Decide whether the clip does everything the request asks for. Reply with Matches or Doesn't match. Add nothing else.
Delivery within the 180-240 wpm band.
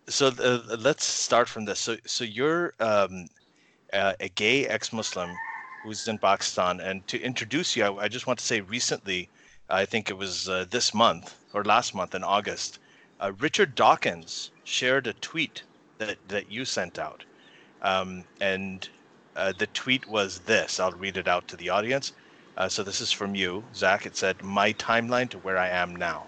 Matches